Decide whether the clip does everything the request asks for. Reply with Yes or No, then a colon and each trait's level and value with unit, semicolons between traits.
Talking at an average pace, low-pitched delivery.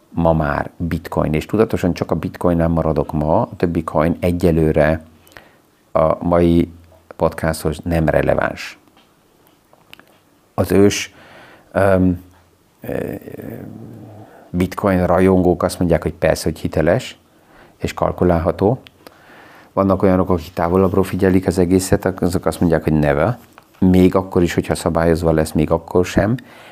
Yes: average, 120 wpm; very low, 85 Hz